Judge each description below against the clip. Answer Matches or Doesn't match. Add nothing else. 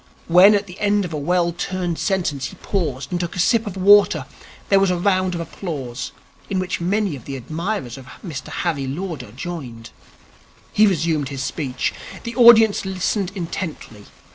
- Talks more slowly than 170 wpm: Doesn't match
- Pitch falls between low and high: Matches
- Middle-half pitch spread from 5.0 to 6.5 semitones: Matches